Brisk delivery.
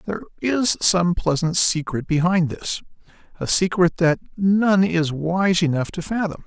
No: average, 150 wpm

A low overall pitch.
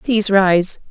No: high, 195 Hz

